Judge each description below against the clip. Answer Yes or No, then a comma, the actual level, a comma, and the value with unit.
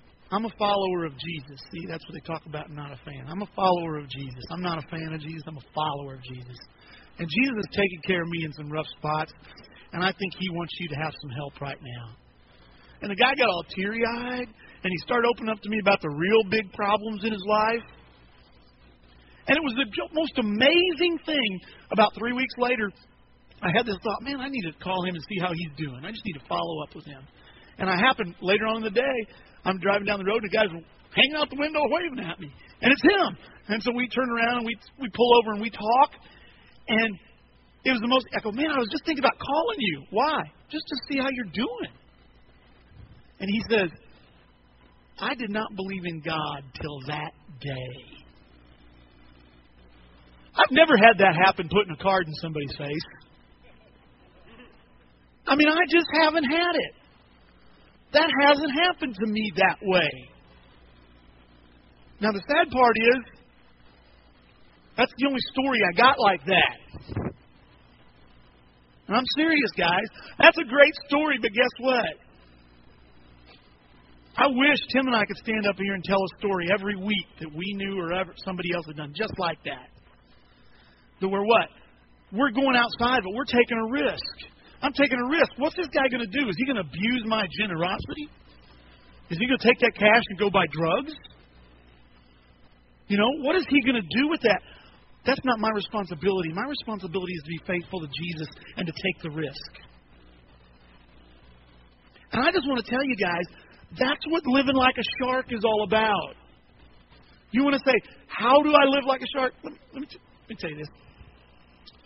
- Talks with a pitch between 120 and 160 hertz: No, high, 190 Hz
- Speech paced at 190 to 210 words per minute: Yes, average, 195 wpm